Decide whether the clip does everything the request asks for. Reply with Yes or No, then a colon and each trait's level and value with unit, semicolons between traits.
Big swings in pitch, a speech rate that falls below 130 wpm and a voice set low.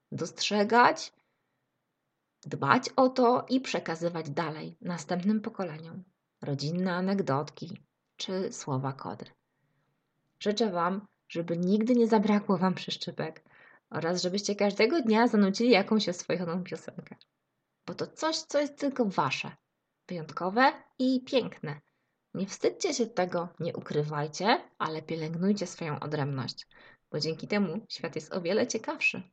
No: wide, 6.0 semitones; average, 120 wpm; medium, 185 Hz